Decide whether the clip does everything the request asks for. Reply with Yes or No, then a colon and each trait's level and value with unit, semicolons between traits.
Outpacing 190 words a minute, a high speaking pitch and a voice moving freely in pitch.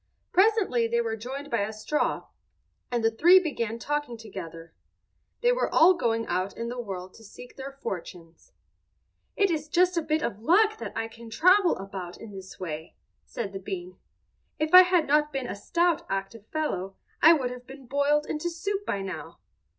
No: average, 185 wpm; high, 245 Hz; wide, 7.9 semitones